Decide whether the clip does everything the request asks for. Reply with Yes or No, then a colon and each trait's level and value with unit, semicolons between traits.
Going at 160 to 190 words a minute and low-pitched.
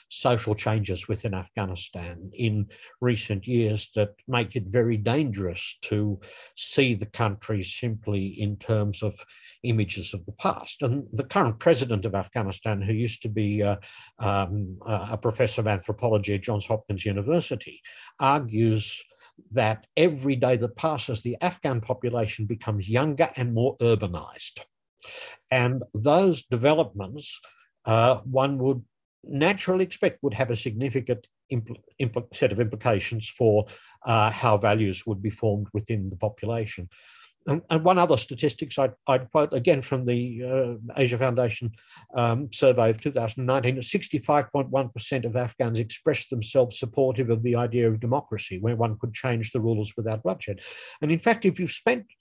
No: average, 150 wpm; low, 115 Hz